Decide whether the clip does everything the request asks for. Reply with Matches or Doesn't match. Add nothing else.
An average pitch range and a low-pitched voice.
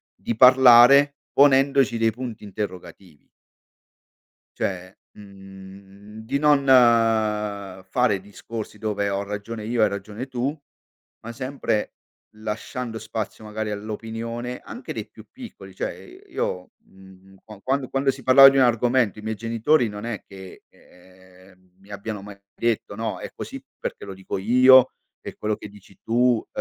Matches